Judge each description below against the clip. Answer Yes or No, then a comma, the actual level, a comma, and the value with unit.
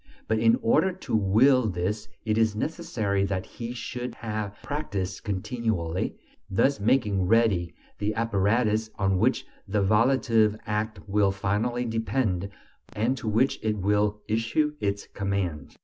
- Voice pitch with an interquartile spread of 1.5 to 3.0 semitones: Yes, average, 2.7 semitones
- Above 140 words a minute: No, slow, 135 wpm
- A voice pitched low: Yes, low, 105 Hz